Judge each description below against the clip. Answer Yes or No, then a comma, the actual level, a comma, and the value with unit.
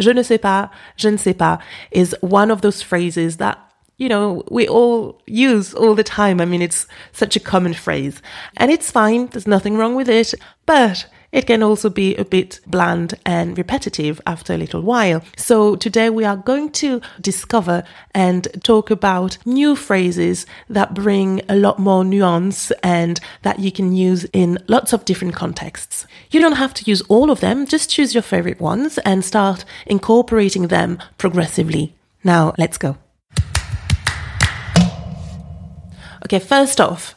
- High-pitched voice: Yes, high, 200 Hz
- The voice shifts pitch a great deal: No, average, 4.2 semitones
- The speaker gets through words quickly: No, average, 165 wpm